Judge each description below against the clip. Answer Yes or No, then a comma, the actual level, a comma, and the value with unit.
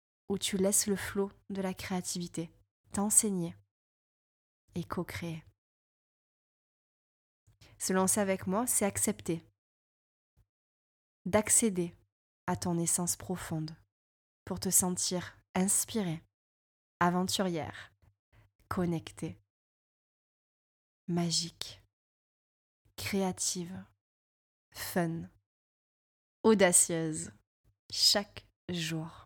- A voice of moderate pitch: Yes, medium, 170 Hz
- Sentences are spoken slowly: Yes, slow, 70 wpm